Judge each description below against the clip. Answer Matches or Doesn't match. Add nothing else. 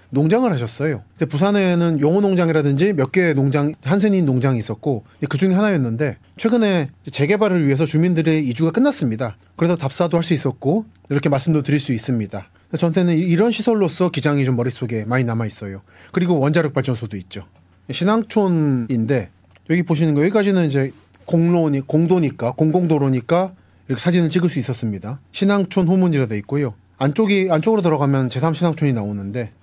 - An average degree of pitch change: Doesn't match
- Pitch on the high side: Doesn't match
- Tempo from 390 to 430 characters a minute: Matches